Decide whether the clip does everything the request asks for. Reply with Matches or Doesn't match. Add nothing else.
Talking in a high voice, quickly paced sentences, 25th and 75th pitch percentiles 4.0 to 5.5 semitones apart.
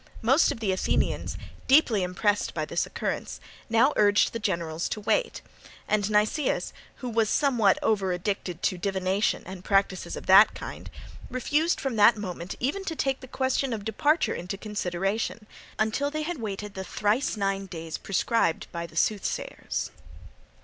Doesn't match